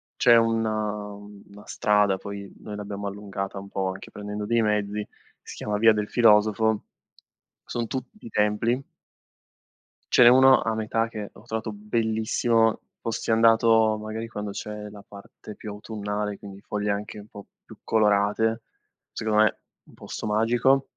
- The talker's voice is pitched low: Yes, low, 105 Hz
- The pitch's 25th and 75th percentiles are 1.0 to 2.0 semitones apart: Yes, narrow, 1.5 semitones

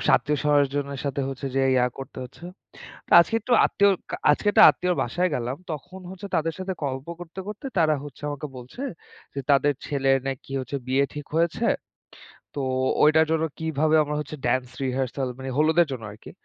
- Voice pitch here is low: No, medium, 145 Hz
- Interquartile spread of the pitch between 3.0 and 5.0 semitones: Yes, average, 3.4 semitones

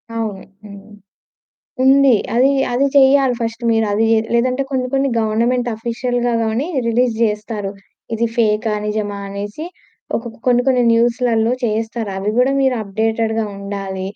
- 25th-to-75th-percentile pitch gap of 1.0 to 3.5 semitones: Yes, narrow, 2.6 semitones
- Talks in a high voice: Yes, high, 230 Hz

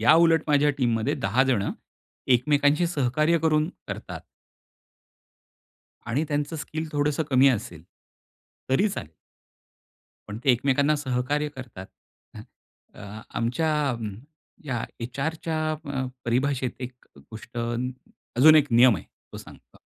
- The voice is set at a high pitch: No, low, 135 Hz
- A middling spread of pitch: Yes, average, 4.1 semitones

